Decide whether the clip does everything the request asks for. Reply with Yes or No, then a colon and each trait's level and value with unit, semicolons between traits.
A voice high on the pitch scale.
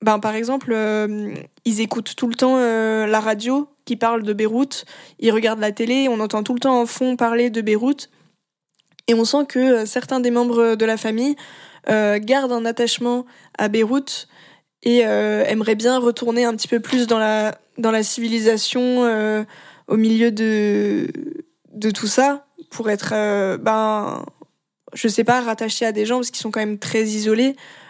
Yes: high, 230 Hz